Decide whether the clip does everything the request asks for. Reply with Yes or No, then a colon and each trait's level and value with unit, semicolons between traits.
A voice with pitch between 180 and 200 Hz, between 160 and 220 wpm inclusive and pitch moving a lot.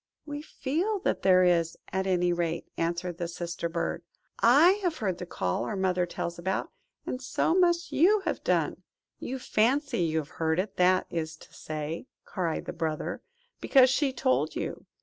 Yes: medium, 185 Hz; average, 175 wpm; wide, 7.8 semitones